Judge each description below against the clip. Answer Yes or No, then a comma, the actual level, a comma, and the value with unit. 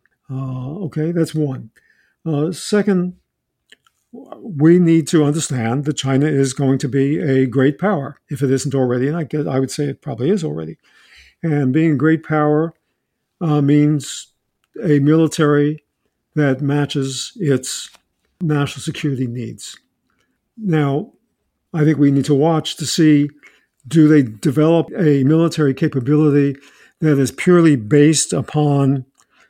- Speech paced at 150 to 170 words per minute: No, slow, 135 wpm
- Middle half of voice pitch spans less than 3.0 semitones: Yes, narrow, 2.5 semitones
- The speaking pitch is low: No, medium, 145 Hz